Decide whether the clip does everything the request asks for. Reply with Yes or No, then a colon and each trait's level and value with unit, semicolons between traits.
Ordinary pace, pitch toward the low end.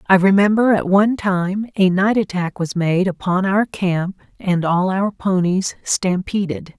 No: average, 160 wpm; high, 190 Hz